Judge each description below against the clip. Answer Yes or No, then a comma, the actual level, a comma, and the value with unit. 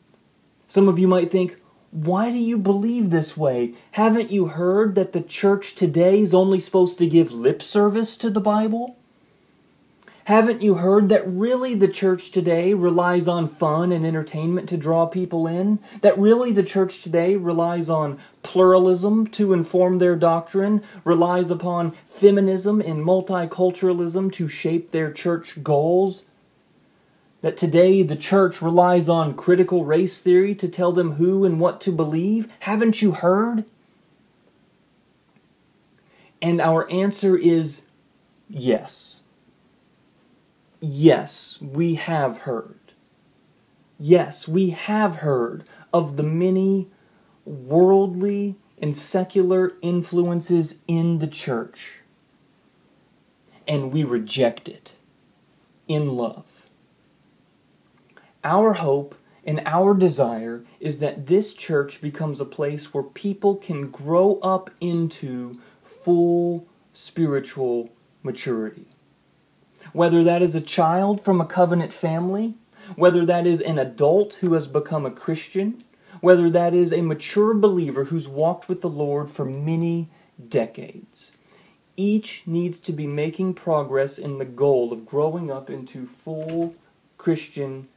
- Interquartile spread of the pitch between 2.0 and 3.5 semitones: Yes, average, 3.2 semitones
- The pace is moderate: No, slow, 125 wpm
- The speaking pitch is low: No, medium, 175 Hz